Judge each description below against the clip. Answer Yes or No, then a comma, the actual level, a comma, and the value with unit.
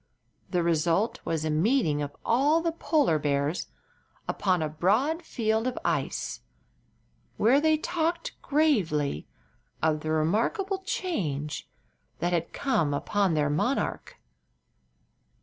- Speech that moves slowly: Yes, slow, 115 wpm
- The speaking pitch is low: No, medium, 185 Hz